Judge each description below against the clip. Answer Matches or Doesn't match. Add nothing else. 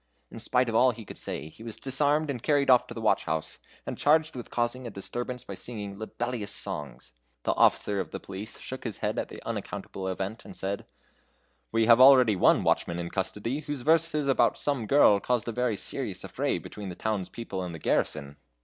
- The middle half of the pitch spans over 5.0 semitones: Doesn't match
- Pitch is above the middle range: Doesn't match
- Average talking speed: Doesn't match